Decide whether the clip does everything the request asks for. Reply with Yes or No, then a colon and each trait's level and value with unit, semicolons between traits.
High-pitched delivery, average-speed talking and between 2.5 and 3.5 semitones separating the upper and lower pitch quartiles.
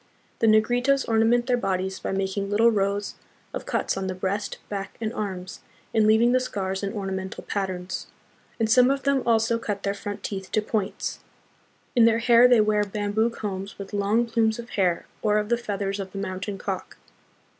Yes: high, 210 Hz; average, 190 wpm; average, 2.9 semitones